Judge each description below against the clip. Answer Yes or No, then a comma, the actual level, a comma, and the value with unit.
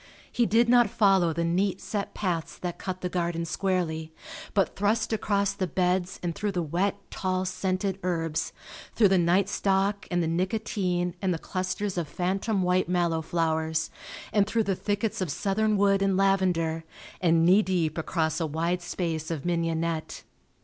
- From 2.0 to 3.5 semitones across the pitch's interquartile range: Yes, average, 2.9 semitones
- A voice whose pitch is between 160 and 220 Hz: Yes, medium, 185 Hz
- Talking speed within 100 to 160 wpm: No, average, 170 wpm